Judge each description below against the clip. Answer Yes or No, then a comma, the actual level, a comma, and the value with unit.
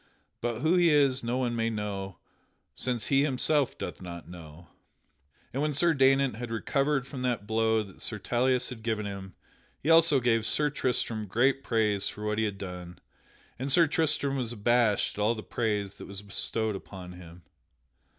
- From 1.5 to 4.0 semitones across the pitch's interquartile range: No, average, 4.7 semitones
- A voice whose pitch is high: No, low, 115 Hz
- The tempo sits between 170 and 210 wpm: Yes, average, 180 wpm